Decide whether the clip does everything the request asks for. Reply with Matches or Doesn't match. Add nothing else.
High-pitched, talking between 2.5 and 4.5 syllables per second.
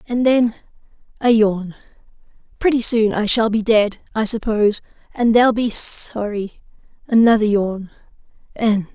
Matches